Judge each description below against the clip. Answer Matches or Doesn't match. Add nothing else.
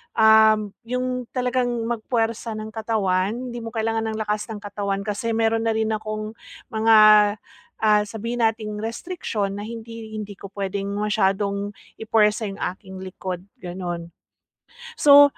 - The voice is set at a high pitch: Matches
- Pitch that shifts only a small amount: Matches